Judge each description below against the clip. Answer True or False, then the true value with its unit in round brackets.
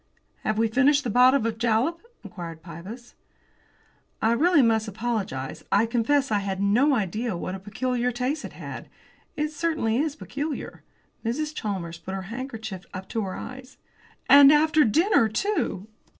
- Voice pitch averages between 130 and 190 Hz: False (230 Hz)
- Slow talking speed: False (155 wpm)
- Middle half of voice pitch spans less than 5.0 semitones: False (5.6 semitones)